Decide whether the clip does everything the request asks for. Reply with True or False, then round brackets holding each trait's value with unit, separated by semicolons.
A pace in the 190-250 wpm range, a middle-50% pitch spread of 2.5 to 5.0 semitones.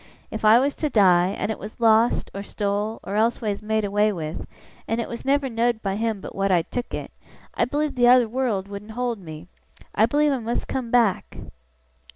True (205 wpm; 3.2 semitones)